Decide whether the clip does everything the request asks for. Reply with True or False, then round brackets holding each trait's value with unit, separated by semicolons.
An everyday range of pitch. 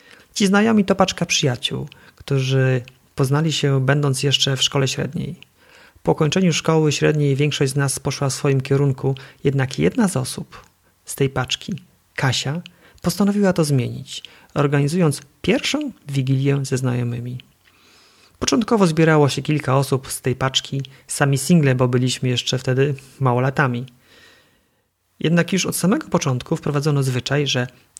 True (3.5 semitones)